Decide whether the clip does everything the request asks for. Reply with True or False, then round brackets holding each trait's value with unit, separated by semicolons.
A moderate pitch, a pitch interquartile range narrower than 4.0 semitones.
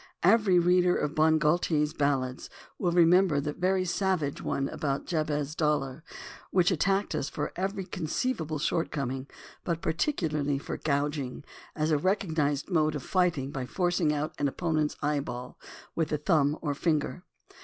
True (155 Hz; 3.6 semitones)